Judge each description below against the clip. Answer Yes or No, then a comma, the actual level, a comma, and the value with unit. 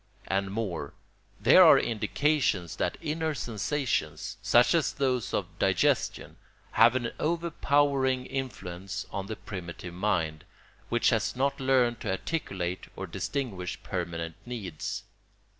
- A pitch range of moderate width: No, wide, 6.4 semitones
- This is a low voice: Yes, low, 115 Hz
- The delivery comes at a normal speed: No, slow, 120 wpm